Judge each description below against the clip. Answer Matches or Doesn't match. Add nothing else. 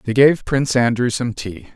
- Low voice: Matches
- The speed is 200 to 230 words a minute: Matches